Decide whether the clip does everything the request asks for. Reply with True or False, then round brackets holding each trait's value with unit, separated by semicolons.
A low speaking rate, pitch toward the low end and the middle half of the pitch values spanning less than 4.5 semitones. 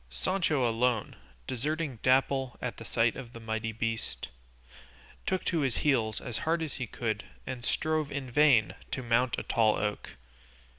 False (160 wpm; 125 Hz; 3.8 semitones)